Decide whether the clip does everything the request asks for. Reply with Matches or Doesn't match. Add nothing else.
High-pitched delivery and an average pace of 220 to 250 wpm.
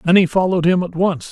Doesn't match